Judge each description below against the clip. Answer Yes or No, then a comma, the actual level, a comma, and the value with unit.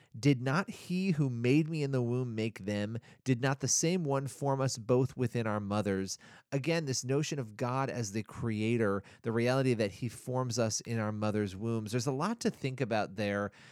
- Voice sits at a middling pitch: No, low, 125 Hz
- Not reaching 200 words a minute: No, fast, 205 wpm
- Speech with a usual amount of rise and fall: Yes, average, 3.7 semitones